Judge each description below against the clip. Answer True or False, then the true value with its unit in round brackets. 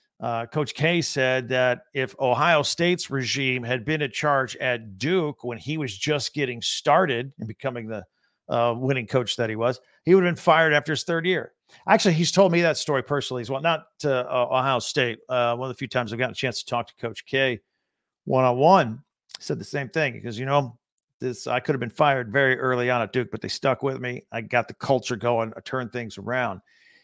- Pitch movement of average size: True (3.4 semitones)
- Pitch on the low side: True (130 Hz)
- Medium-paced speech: False (225 wpm)